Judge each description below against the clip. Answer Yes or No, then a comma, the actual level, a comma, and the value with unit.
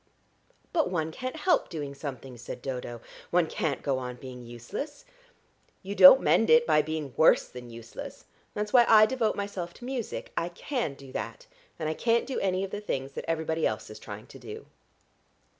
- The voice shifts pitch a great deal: Yes, wide, 8.8 semitones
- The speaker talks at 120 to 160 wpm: No, average, 190 wpm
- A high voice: No, medium, 160 Hz